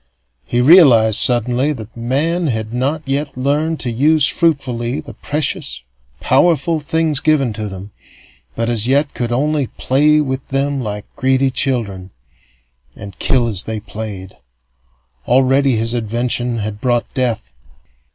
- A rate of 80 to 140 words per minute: Yes, slow, 135 wpm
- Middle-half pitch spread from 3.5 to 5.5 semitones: Yes, average, 4.1 semitones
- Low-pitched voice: Yes, low, 125 Hz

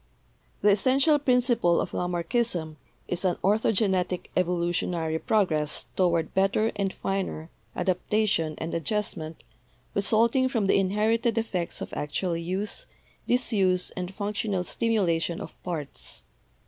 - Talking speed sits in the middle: No, slow, 115 wpm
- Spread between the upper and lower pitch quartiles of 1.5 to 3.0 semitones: No, average, 4.1 semitones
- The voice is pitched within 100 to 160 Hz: No, high, 190 Hz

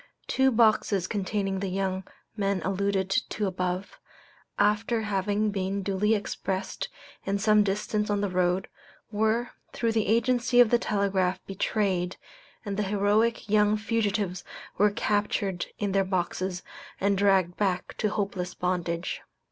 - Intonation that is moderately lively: No, narrow, 2.0 semitones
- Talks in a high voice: Yes, high, 200 Hz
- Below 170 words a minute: Yes, slow, 135 wpm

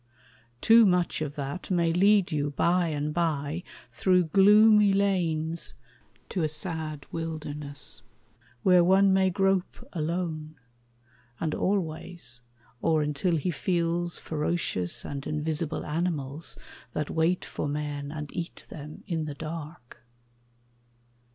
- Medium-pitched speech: Yes, medium, 165 Hz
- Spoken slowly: Yes, slow, 120 wpm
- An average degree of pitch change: Yes, average, 3.1 semitones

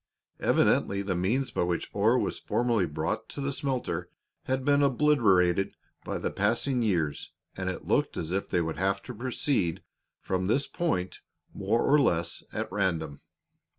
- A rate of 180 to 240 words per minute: No, average, 160 wpm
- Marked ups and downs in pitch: Yes, wide, 6.7 semitones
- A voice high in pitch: No, low, 100 Hz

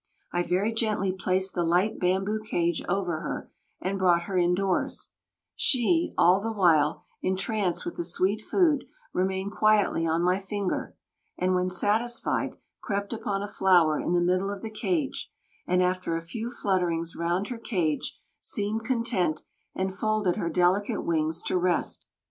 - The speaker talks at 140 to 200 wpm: Yes, average, 155 wpm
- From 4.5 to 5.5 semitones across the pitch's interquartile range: No, average, 3.2 semitones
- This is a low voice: No, high, 190 Hz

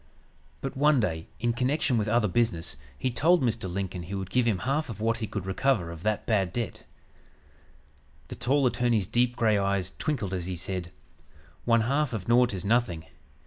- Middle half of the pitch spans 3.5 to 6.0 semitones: Yes, average, 4.5 semitones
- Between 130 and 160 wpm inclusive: No, average, 185 wpm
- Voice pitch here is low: Yes, low, 110 Hz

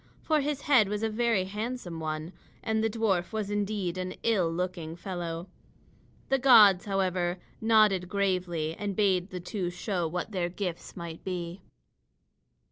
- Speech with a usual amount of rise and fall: Yes, average, 3.4 semitones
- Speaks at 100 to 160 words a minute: Yes, average, 150 wpm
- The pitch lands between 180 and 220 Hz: Yes, high, 190 Hz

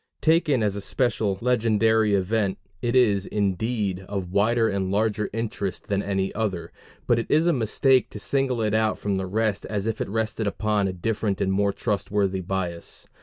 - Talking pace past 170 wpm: Yes, average, 180 wpm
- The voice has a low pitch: Yes, low, 105 Hz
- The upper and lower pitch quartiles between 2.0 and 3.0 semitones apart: Yes, narrow, 2.5 semitones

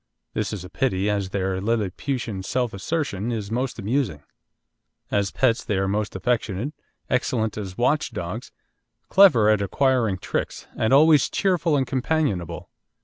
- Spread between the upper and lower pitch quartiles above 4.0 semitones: Yes, average, 5.3 semitones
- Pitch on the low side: Yes, low, 110 Hz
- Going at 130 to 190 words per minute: Yes, average, 145 wpm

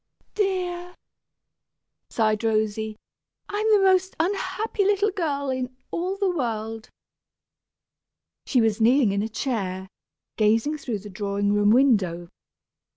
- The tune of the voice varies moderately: No, wide, 9.0 semitones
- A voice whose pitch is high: Yes, high, 245 Hz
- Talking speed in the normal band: No, slow, 115 wpm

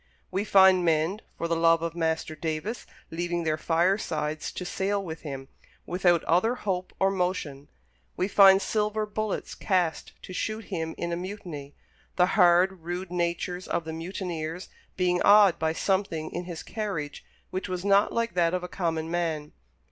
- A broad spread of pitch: No, average, 2.8 semitones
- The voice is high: No, medium, 175 Hz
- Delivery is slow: No, average, 165 wpm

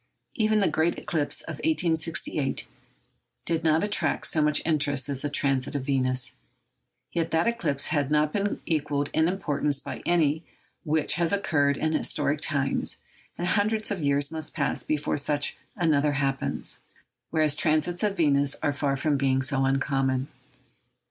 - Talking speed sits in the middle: Yes, average, 155 wpm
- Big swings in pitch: No, average, 2.8 semitones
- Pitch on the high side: No, medium, 150 Hz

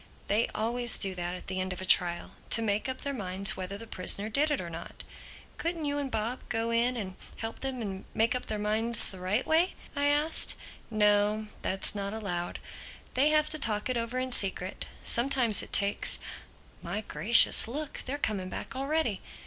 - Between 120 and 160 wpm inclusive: No, average, 190 wpm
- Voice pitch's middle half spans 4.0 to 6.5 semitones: Yes, average, 4.7 semitones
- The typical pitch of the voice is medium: No, high, 220 Hz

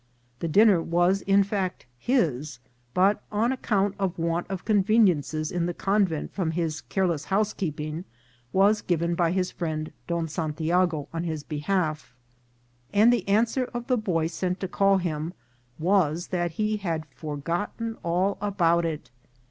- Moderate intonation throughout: Yes, average, 3.6 semitones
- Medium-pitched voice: Yes, medium, 175 Hz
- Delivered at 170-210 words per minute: No, average, 150 wpm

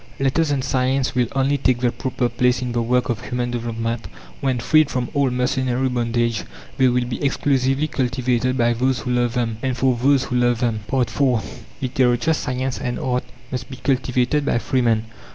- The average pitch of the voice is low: Yes, low, 125 Hz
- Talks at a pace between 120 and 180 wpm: No, average, 190 wpm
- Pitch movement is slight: Yes, narrow, 1.6 semitones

